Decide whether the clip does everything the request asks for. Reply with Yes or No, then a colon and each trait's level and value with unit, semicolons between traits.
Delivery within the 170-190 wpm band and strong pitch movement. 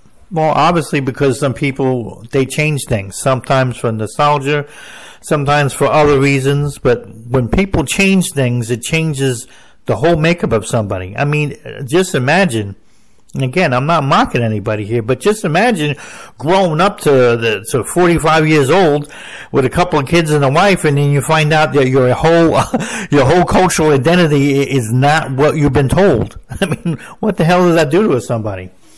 No: average, 180 wpm; average, 4.2 semitones